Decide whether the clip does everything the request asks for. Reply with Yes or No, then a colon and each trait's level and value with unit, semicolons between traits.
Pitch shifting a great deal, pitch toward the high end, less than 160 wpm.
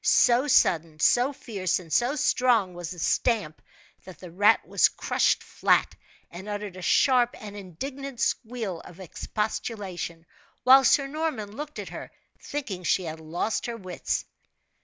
Yes: wide, 5.8 semitones; high, 205 Hz; average, 150 wpm